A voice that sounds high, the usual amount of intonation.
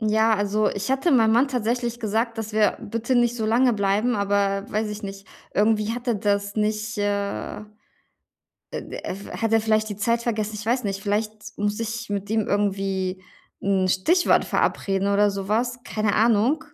No: high, 215 Hz; narrow, 2.2 semitones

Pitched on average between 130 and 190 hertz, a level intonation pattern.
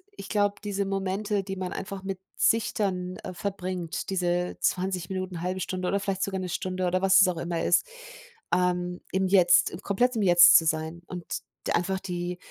Yes: medium, 185 Hz; narrow, 1.5 semitones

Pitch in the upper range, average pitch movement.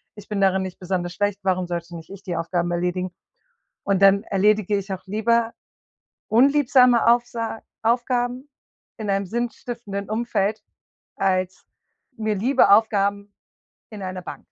Yes: high, 200 Hz; average, 3.6 semitones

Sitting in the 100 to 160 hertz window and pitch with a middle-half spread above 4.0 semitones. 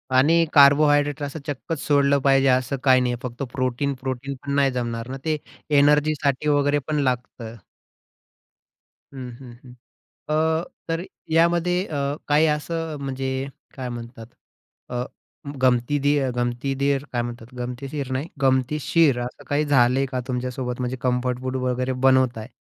No: low, 135 Hz; narrow, 2.6 semitones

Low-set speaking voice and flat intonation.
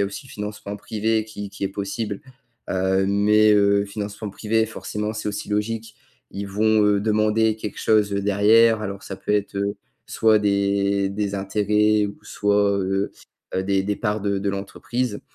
Yes: low, 105 Hz; narrow, 1.3 semitones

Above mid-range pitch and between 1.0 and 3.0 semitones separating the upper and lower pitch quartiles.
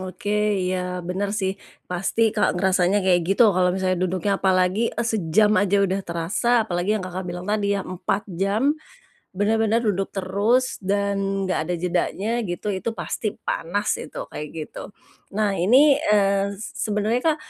Yes: high, 195 Hz; narrow, 2.5 semitones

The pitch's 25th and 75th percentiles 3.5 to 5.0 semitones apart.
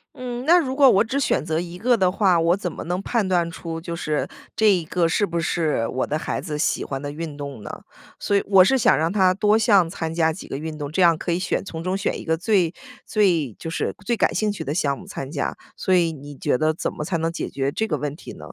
Yes: average, 4.1 semitones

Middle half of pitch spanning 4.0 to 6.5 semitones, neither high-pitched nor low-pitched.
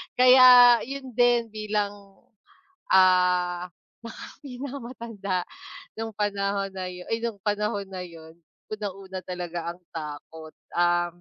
No: average, 4.3 semitones; high, 200 Hz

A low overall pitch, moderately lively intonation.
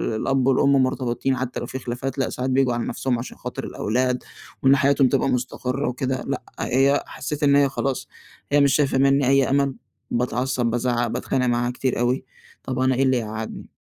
No: low, 130 Hz; narrow, 1.7 semitones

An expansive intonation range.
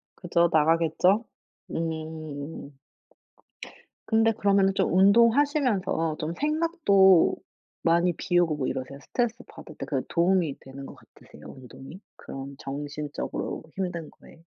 No: average, 4.8 semitones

